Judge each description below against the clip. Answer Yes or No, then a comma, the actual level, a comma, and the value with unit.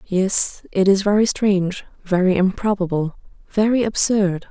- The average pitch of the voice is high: Yes, high, 195 Hz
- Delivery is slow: Yes, slow, 120 wpm